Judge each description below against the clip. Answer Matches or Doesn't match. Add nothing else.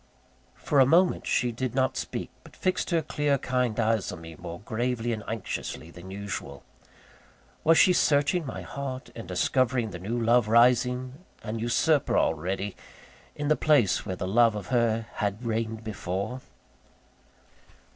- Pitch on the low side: Matches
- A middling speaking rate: Matches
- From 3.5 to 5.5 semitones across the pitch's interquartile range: Matches